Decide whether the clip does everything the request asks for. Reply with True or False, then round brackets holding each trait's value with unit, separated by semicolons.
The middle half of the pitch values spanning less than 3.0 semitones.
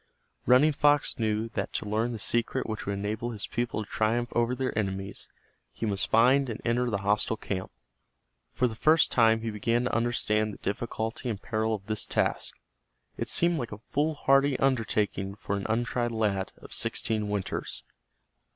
True (2.6 semitones)